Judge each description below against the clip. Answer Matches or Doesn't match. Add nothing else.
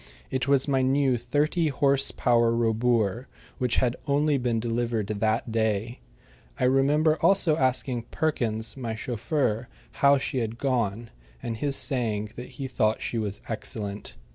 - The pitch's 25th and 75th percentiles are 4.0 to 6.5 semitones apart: Doesn't match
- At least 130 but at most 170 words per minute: Matches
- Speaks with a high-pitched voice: Doesn't match